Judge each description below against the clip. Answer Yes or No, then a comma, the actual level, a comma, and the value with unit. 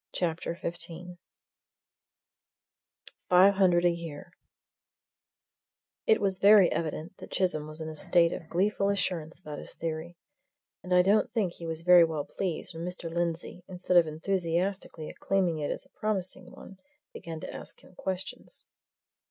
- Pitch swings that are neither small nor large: No, narrow, 2.3 semitones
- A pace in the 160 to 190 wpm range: No, average, 150 wpm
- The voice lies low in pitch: No, medium, 175 Hz